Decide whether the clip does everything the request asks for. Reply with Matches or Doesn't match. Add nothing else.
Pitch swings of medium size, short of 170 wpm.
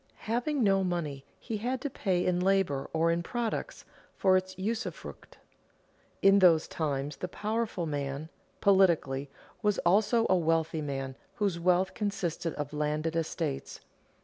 Matches